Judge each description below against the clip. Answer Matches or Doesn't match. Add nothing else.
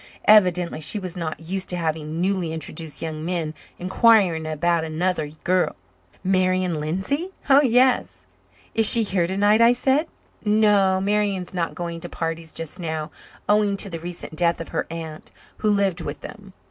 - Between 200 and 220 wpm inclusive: Doesn't match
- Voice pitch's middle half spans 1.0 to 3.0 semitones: Doesn't match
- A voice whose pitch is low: Doesn't match